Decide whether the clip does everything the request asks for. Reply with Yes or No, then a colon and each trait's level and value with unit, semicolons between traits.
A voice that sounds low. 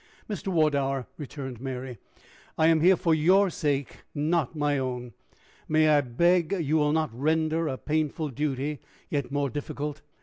No: medium, 150 Hz